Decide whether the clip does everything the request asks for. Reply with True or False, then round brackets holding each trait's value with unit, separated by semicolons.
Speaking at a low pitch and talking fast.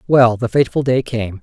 True (120 Hz; 210 wpm)